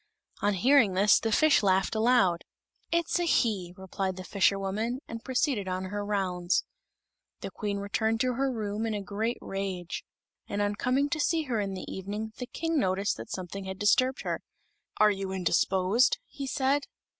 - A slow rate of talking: No, average, 175 wpm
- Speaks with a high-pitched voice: Yes, high, 205 Hz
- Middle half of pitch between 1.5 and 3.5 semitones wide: No, average, 4.6 semitones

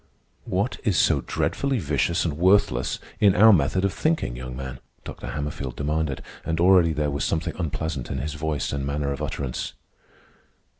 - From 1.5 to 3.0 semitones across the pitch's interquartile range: No, average, 4.8 semitones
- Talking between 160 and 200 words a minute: Yes, average, 165 wpm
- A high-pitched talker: No, very low, 75 Hz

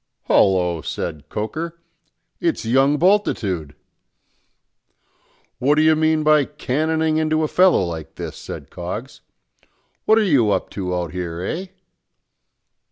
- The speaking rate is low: Yes, slow, 125 wpm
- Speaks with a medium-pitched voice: Yes, medium, 145 Hz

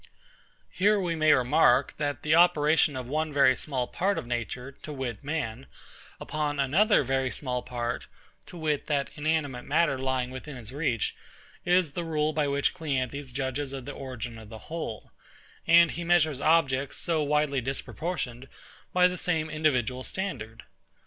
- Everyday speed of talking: Yes, average, 160 wpm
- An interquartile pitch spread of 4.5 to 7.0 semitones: No, average, 3.6 semitones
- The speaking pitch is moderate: Yes, medium, 145 Hz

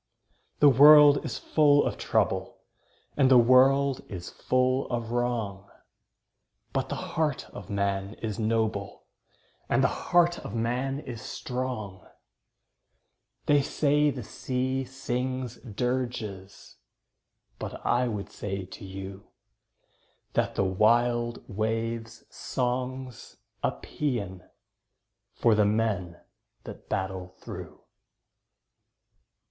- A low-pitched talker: Yes, low, 120 Hz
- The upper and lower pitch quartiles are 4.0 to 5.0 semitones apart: Yes, average, 4.3 semitones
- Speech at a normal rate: No, slow, 105 wpm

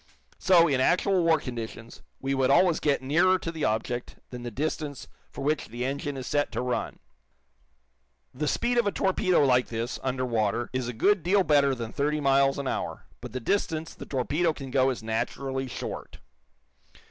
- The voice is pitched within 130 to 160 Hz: Yes, low, 135 Hz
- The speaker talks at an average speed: Yes, average, 185 wpm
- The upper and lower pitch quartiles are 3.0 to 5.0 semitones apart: Yes, average, 4.2 semitones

